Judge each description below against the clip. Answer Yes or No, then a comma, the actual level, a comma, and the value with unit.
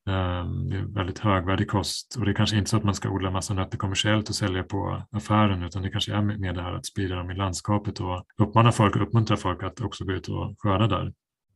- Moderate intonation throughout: No, narrow, 2.1 semitones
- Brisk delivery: Yes, fast, 245 wpm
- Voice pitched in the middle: No, low, 100 Hz